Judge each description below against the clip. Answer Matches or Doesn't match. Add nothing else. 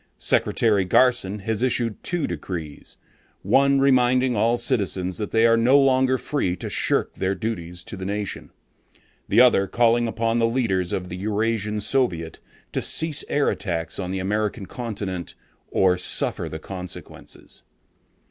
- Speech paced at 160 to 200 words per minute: Doesn't match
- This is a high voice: Doesn't match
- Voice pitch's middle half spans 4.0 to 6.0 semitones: Matches